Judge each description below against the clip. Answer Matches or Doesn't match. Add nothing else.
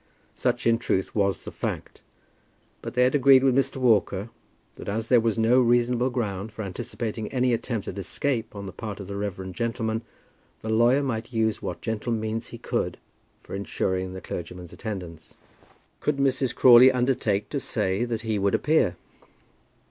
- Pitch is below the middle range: Matches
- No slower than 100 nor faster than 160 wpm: Doesn't match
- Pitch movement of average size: Matches